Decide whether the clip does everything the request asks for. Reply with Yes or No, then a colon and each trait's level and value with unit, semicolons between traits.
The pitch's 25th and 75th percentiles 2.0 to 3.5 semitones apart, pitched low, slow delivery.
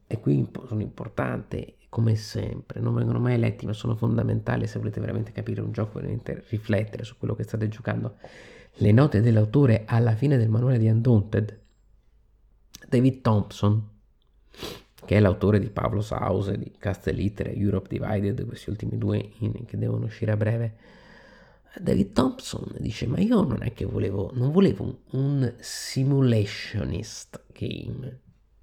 No: narrow, 2.4 semitones; low, 110 Hz; average, 145 wpm